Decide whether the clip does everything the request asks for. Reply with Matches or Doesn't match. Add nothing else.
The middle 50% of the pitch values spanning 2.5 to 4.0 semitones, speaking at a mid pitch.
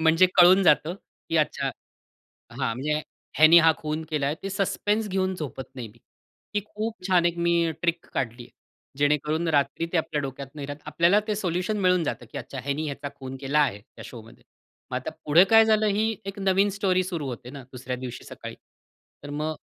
Doesn't match